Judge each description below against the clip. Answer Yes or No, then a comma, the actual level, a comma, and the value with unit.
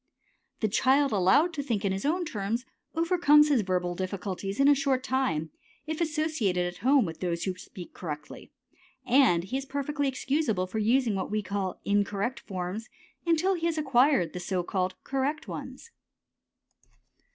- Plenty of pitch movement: Yes, wide, 7.3 semitones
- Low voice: No, high, 230 Hz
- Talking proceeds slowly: No, average, 165 wpm